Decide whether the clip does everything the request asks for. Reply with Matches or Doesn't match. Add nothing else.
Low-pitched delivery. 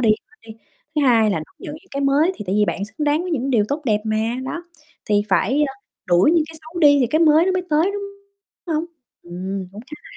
Doesn't match